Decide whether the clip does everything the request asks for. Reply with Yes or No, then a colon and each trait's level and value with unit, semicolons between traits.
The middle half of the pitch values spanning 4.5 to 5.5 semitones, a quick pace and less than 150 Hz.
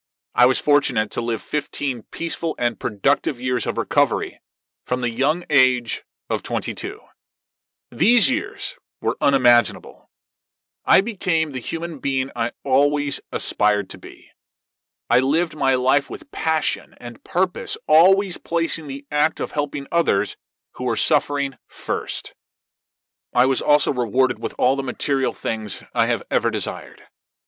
No: average, 5.2 semitones; average, 140 wpm; medium, 140 Hz